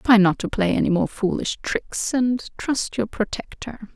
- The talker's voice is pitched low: No, high, 220 Hz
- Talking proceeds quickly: No, average, 180 wpm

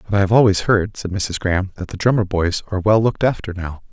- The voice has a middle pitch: No, low, 100 Hz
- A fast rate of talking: Yes, fast, 260 wpm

